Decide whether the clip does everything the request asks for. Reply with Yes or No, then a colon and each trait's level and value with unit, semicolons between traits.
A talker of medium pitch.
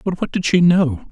Yes: medium, 165 Hz